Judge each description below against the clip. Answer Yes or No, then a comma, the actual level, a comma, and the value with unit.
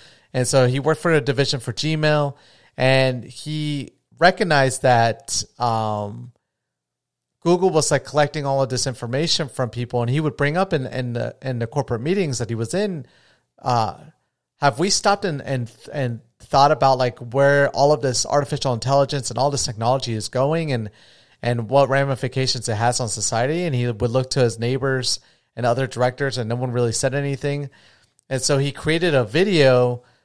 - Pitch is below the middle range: Yes, low, 130 Hz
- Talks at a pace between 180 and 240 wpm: Yes, average, 185 wpm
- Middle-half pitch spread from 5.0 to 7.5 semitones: No, average, 2.9 semitones